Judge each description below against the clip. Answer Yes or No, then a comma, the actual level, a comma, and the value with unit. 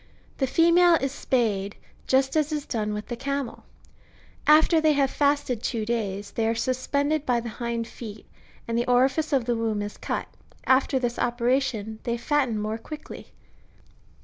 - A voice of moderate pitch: No, high, 245 Hz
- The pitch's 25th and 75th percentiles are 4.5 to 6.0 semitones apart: No, average, 3.8 semitones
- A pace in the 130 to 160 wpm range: No, average, 175 wpm